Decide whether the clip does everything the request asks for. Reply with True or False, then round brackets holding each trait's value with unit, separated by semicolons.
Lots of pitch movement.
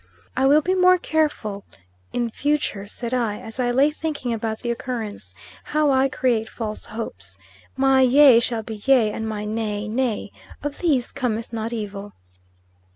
False (3.9 semitones)